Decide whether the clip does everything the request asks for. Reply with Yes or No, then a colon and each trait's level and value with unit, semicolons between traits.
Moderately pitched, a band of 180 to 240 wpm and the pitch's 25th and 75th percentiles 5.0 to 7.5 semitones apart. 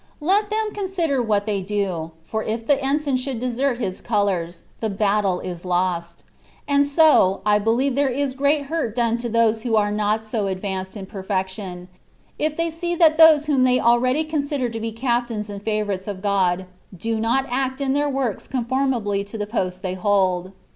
No: high, 225 Hz; average, 190 wpm; wide, 5.5 semitones